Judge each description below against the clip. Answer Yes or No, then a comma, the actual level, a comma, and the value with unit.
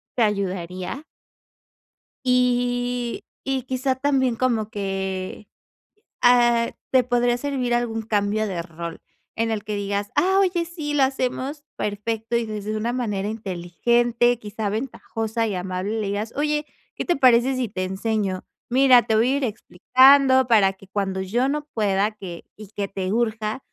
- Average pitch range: Yes, average, 3.8 semitones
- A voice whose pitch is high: Yes, high, 225 Hz